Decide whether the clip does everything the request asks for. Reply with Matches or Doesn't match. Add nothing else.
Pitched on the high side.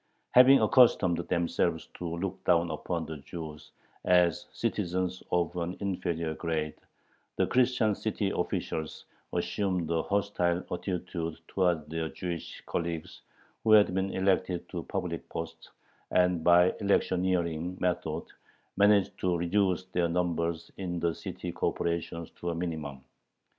Doesn't match